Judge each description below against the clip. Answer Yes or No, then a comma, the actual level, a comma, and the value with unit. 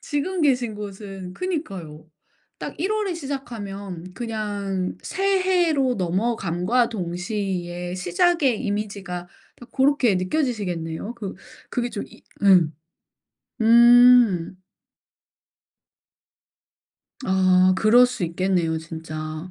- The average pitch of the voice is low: No, high, 205 Hz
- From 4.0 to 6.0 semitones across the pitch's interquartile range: Yes, wide, 5.5 semitones